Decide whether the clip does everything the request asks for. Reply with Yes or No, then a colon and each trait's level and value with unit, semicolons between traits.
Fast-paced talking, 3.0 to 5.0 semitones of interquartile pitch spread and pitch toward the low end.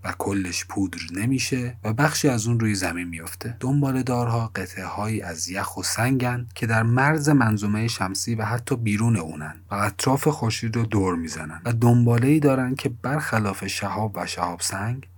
Yes: fast, 175 wpm; average, 4.3 semitones; low, 110 Hz